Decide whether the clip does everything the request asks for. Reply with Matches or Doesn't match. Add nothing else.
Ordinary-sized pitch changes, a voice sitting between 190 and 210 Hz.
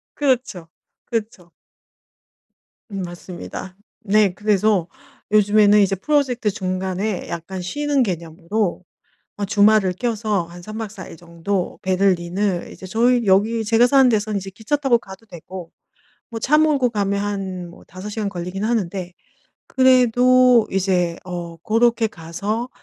Matches